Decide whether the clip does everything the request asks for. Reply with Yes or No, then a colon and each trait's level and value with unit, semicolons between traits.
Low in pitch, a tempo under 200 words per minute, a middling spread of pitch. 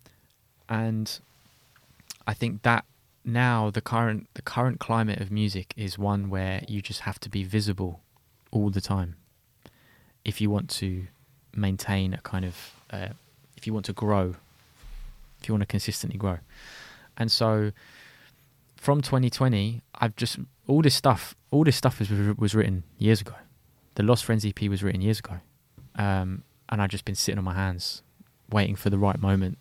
Yes: low, 105 Hz; average, 170 wpm; average, 3.4 semitones